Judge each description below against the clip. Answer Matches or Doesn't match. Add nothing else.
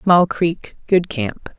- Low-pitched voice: Doesn't match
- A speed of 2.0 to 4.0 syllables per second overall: Matches